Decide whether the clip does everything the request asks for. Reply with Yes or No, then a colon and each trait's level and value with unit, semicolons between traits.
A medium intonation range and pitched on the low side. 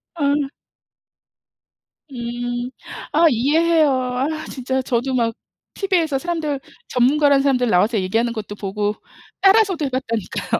No: average, 4.3 semitones; very high, 260 Hz